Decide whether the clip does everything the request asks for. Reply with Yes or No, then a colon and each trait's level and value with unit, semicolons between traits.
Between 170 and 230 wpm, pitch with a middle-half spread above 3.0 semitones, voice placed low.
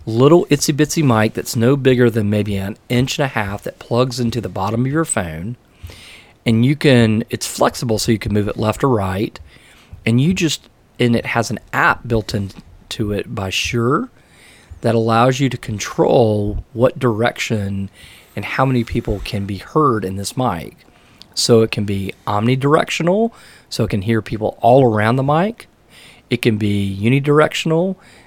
Yes: average, 175 wpm; average, 3.6 semitones; low, 115 Hz